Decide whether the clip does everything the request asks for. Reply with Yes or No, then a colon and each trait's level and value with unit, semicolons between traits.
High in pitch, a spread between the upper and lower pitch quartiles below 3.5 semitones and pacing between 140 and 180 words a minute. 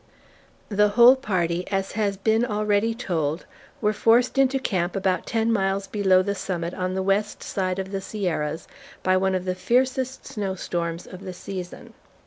Yes: high, 195 Hz; average, 2.8 semitones; average, 170 wpm